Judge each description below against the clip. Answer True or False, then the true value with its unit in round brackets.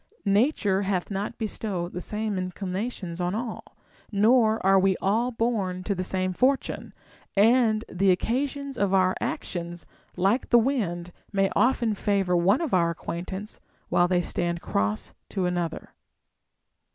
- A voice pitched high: True (195 Hz)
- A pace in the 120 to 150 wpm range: True (140 wpm)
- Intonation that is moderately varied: True (3.7 semitones)